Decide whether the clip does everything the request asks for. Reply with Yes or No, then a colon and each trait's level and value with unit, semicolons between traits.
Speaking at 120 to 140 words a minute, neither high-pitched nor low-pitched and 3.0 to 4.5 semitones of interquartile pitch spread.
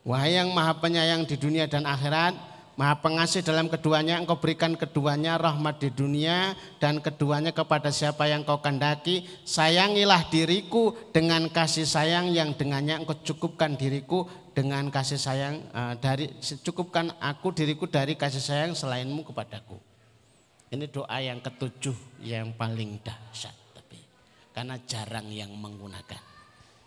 Yes: average, 135 wpm; medium, 150 Hz; average, 3.8 semitones